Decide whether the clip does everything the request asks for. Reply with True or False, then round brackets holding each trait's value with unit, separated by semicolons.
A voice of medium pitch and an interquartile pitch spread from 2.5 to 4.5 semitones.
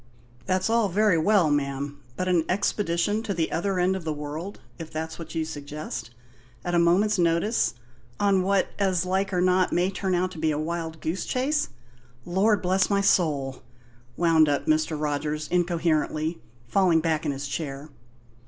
True (170 Hz; 3.4 semitones)